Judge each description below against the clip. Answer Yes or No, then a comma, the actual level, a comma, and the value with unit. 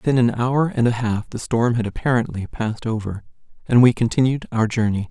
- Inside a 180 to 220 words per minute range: Yes, average, 200 wpm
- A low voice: Yes, low, 115 Hz